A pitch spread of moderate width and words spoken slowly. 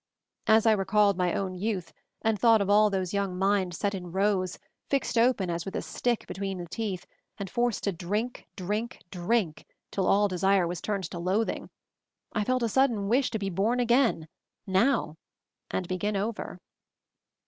No: average, 3.3 semitones; average, 185 wpm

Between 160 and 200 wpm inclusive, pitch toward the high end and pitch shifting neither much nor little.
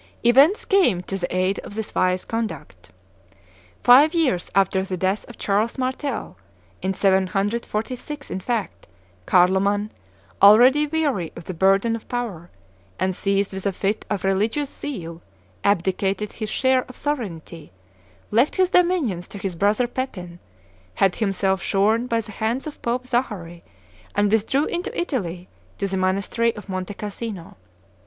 No: average, 145 wpm; high, 205 Hz; average, 4.5 semitones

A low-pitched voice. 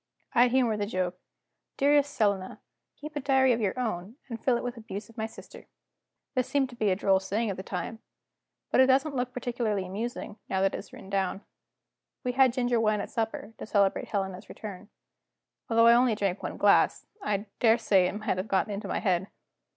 No: high, 220 Hz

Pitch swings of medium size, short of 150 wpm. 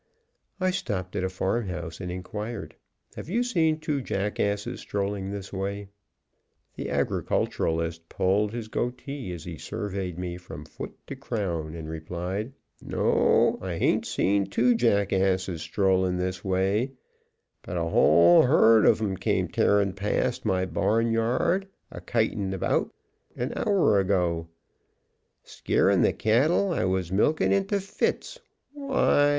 Yes: average, 4.6 semitones; slow, 135 wpm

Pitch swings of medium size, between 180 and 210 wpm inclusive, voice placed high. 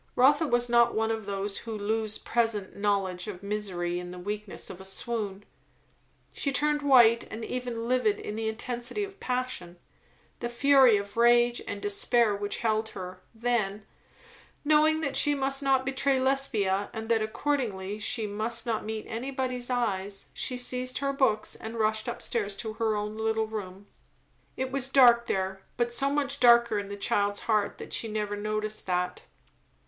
No: average, 3.6 semitones; average, 170 wpm; high, 225 Hz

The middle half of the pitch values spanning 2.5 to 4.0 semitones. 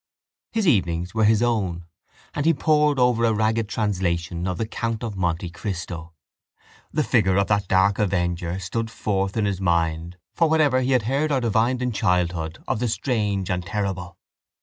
No: average, 4.8 semitones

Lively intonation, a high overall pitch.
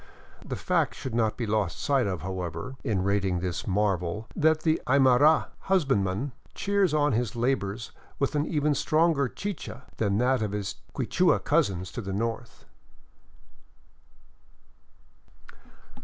No: wide, 6.5 semitones; low, 115 Hz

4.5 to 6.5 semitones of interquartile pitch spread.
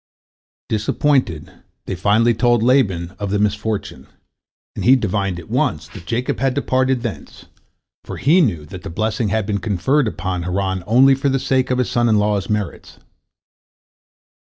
Yes: average, 5.0 semitones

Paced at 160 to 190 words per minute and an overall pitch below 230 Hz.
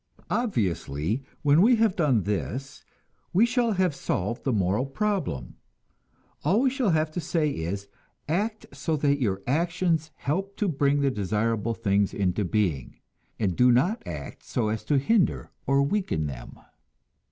No: average, 150 wpm; medium, 140 Hz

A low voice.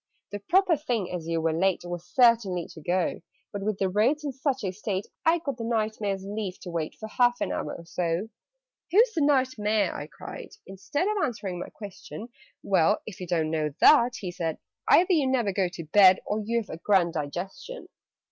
No: high, 205 Hz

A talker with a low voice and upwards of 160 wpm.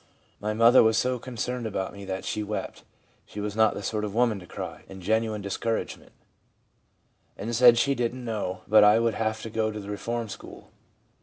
Yes: low, 110 Hz; average, 200 wpm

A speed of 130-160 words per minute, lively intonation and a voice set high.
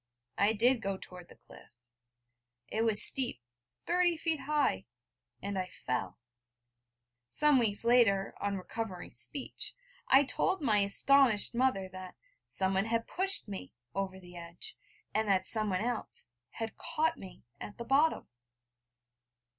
Yes: slow, 135 wpm; wide, 5.7 semitones; high, 220 Hz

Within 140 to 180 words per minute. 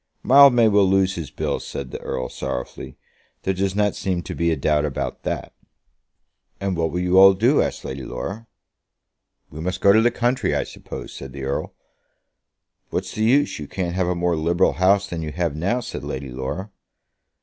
No: average, 195 wpm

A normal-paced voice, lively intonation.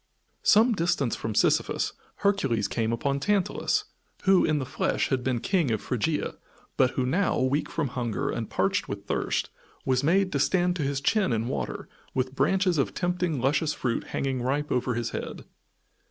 Yes: average, 175 wpm; wide, 5.9 semitones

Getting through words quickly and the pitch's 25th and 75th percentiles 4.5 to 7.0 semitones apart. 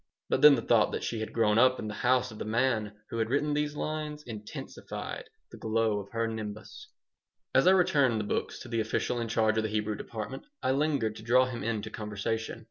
No: fast, 220 wpm; average, 3.0 semitones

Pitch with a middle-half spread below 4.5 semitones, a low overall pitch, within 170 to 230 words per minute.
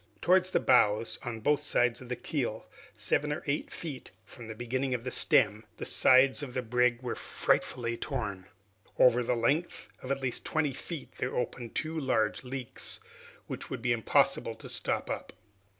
Yes: average, 2.8 semitones; low, 125 Hz; average, 180 wpm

